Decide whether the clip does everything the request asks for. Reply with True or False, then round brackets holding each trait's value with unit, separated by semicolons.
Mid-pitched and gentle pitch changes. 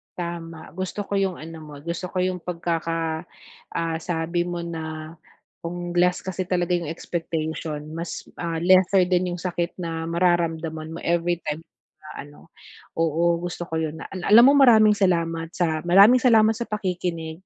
True (170 Hz; 1.9 semitones)